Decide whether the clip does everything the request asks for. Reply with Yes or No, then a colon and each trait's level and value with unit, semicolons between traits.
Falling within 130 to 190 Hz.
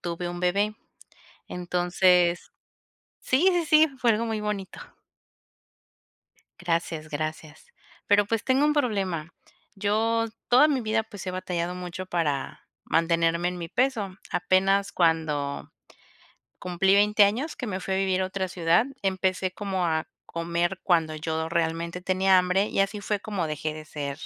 Yes: medium, 185 Hz